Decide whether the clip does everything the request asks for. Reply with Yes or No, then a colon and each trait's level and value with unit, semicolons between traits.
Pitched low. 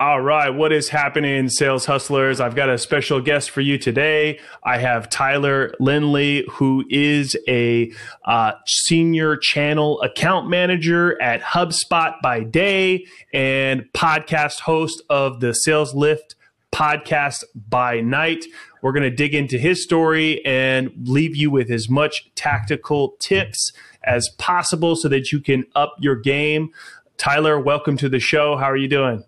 No: medium, 145 Hz